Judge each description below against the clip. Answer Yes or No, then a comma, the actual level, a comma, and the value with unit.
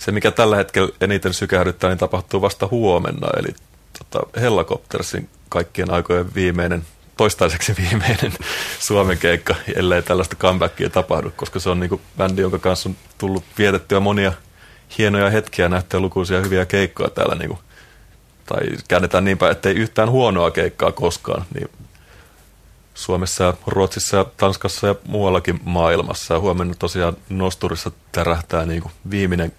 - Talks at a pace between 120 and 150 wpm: Yes, average, 140 wpm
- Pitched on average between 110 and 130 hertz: No, very low, 95 Hz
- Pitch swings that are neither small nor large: No, narrow, 2.0 semitones